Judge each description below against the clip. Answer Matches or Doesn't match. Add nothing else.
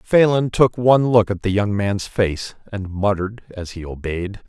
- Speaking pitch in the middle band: Doesn't match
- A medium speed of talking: Matches